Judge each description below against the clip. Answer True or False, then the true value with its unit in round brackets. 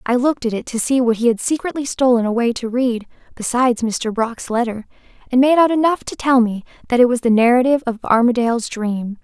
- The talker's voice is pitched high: True (240 Hz)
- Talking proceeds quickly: True (215 wpm)